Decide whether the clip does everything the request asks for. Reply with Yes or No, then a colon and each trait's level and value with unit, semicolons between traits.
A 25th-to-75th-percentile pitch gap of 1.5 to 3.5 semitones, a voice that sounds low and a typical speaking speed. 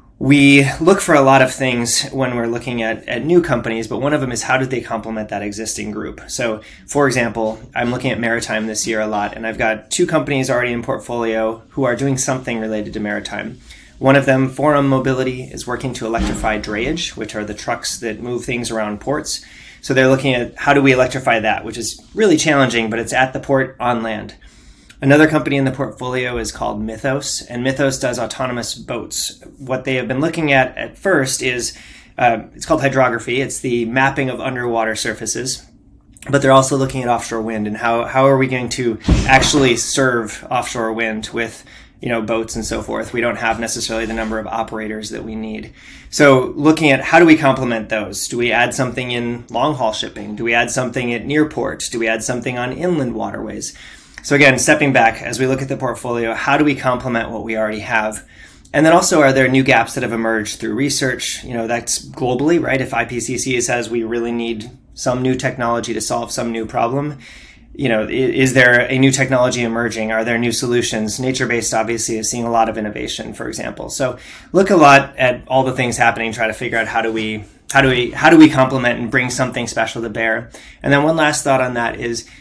No: average, 2.8 semitones; low, 120 Hz; fast, 215 wpm